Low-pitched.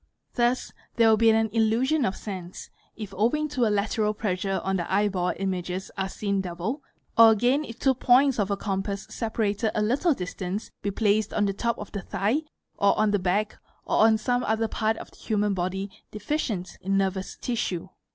No: high, 210 Hz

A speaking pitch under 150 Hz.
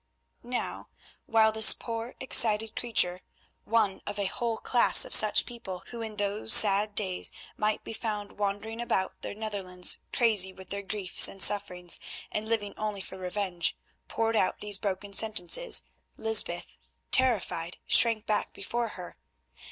No: high, 210 Hz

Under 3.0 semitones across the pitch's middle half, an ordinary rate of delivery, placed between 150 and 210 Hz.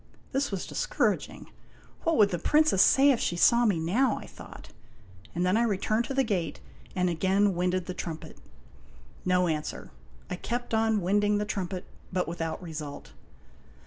No: average, 4.2 semitones; average, 165 wpm; high, 190 Hz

